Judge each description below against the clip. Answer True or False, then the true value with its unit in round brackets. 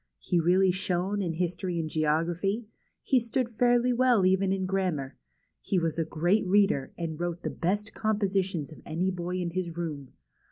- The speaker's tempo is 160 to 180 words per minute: True (170 wpm)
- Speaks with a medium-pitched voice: True (180 Hz)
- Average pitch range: True (3.0 semitones)